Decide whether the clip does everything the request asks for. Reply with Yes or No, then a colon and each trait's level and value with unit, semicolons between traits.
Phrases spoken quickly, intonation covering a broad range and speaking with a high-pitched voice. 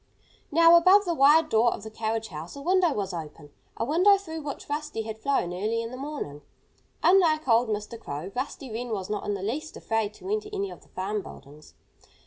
Yes: fast, 210 wpm; wide, 7.3 semitones; high, 235 Hz